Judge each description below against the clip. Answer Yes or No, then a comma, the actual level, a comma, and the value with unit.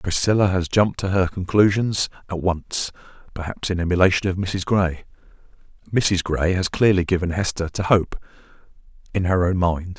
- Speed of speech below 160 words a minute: Yes, average, 150 wpm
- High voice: No, very low, 90 Hz